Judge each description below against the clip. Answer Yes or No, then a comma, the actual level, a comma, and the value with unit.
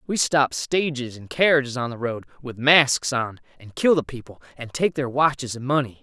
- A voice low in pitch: Yes, low, 130 Hz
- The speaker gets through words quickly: Yes, fast, 210 wpm